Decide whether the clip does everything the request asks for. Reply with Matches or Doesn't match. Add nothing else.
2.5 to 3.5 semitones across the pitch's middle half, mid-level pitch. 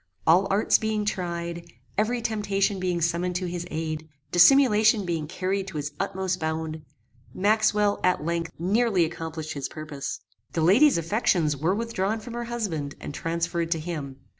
Doesn't match